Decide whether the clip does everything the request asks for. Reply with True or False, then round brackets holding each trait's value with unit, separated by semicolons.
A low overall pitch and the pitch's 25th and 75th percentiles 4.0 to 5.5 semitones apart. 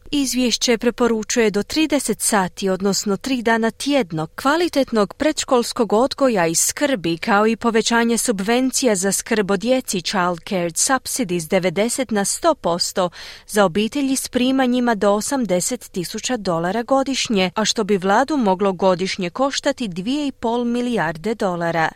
False (225 Hz; 4.8 semitones)